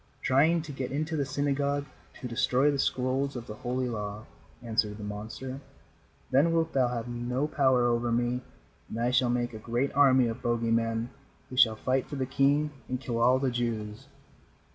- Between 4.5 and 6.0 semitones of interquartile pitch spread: No, average, 2.7 semitones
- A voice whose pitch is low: Yes, low, 125 Hz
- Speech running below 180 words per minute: No, average, 185 wpm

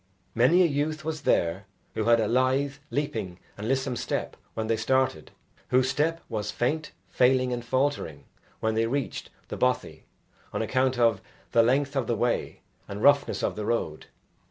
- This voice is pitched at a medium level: No, low, 125 Hz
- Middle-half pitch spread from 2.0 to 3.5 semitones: No, average, 3.9 semitones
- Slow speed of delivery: No, average, 170 wpm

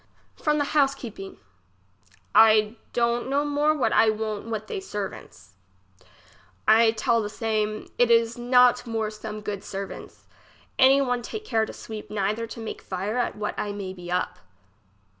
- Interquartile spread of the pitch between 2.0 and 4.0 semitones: Yes, average, 2.7 semitones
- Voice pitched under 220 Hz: No, high, 225 Hz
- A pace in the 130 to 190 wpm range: Yes, average, 165 wpm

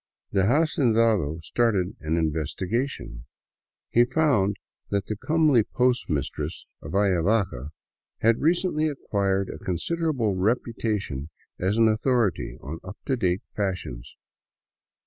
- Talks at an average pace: No, slow, 115 wpm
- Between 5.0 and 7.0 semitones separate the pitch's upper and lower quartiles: Yes, average, 5.3 semitones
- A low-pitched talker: Yes, low, 105 Hz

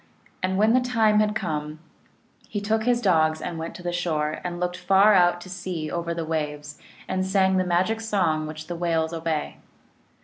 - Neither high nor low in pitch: Yes, medium, 175 Hz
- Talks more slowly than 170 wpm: No, average, 195 wpm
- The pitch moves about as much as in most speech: Yes, average, 3.5 semitones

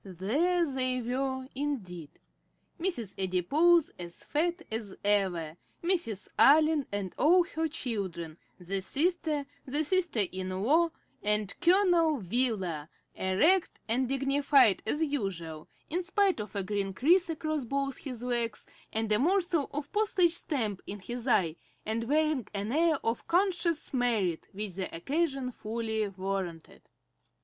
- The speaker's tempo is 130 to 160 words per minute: Yes, slow, 135 wpm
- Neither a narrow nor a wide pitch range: No, wide, 8.0 semitones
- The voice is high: Yes, very high, 250 Hz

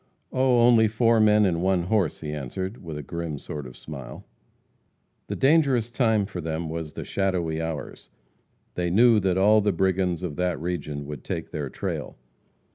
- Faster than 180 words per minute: No, average, 175 wpm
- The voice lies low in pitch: Yes, very low, 90 Hz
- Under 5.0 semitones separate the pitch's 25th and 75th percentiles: No, average, 5.3 semitones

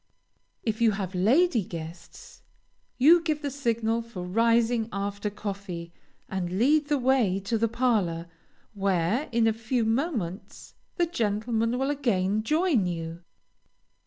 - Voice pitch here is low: No, high, 225 Hz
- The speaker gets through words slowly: Yes, slow, 130 wpm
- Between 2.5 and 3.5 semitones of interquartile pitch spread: No, average, 4.7 semitones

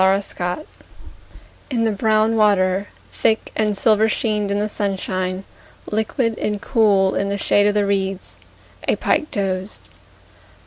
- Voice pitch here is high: Yes, high, 205 Hz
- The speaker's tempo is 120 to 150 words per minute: Yes, average, 140 wpm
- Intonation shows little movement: Yes, narrow, 2.1 semitones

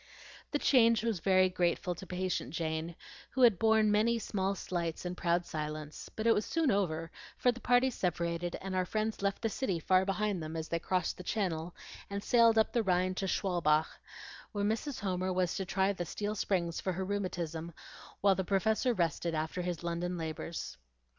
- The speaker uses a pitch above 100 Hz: Yes, medium, 185 Hz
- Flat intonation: No, average, 3.7 semitones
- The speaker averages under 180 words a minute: No, average, 190 wpm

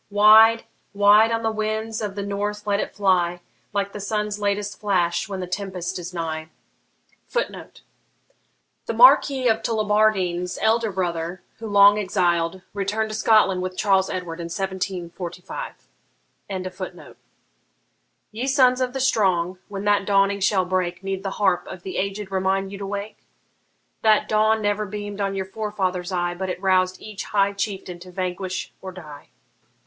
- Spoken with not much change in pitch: Yes, narrow, 2.3 semitones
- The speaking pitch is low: No, high, 195 Hz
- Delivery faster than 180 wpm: No, average, 155 wpm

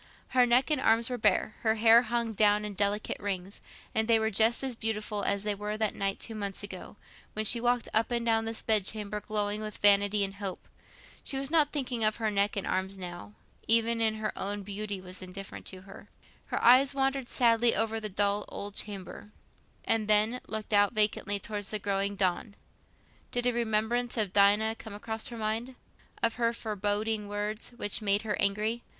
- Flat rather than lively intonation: Yes, narrow, 2.1 semitones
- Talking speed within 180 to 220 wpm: Yes, average, 195 wpm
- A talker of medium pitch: No, high, 215 Hz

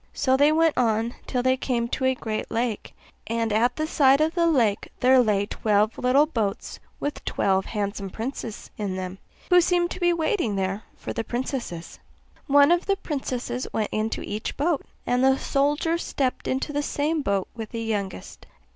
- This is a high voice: Yes, very high, 250 Hz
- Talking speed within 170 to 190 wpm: Yes, average, 180 wpm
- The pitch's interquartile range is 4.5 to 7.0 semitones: Yes, average, 5.2 semitones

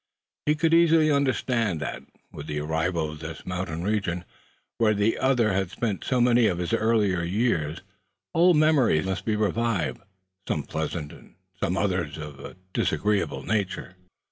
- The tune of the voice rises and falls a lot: Yes, wide, 5.7 semitones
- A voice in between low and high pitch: No, low, 100 Hz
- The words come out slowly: No, average, 150 wpm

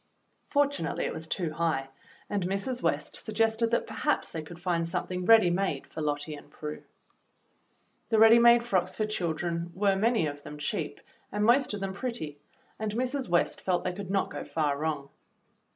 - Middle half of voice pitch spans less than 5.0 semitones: No, wide, 5.6 semitones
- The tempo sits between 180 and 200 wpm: Yes, average, 185 wpm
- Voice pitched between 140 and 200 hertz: Yes, medium, 185 Hz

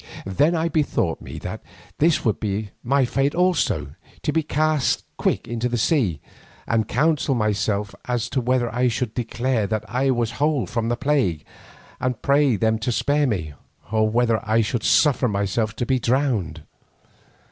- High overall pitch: No, low, 120 Hz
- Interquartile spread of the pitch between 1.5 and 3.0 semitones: No, average, 4.3 semitones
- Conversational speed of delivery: Yes, average, 175 wpm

